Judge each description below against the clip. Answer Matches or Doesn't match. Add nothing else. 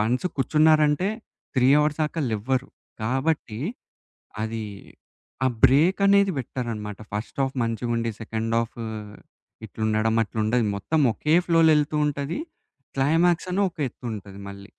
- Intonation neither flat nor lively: Doesn't match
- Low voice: Matches